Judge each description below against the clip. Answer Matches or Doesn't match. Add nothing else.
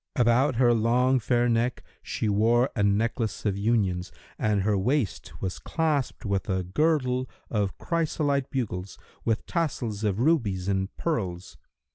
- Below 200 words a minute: Matches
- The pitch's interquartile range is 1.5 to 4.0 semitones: Doesn't match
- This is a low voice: Matches